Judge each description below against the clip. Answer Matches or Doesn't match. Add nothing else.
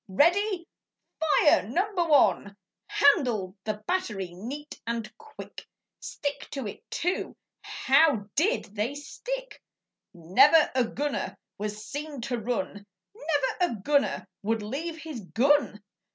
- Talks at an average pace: Doesn't match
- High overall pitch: Matches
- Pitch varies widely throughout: Matches